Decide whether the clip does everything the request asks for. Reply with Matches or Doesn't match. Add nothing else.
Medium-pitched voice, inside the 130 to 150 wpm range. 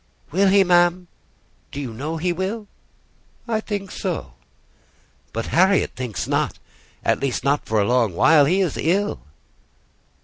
Matches